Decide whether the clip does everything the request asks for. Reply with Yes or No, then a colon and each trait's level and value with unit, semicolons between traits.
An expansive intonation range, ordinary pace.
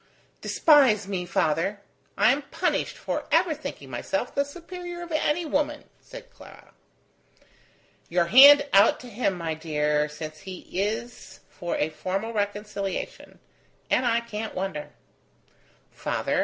No: wide, 8.1 semitones; slow, 130 wpm